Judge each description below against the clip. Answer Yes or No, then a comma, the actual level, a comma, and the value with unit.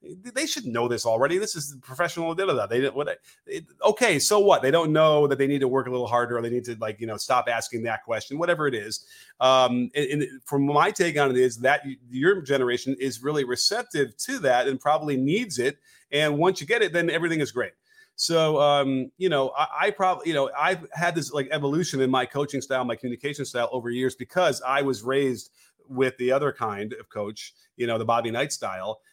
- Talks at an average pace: No, fast, 235 wpm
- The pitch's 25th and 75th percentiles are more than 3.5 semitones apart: Yes, average, 4.8 semitones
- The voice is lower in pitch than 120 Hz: No, medium, 140 Hz